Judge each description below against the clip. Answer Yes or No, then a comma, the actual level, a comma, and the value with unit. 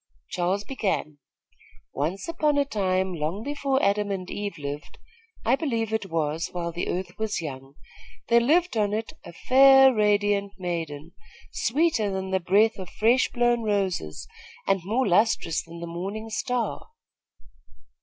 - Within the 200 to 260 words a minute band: No, average, 145 wpm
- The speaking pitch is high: Yes, high, 200 Hz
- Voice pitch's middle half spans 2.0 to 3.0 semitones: No, average, 5.0 semitones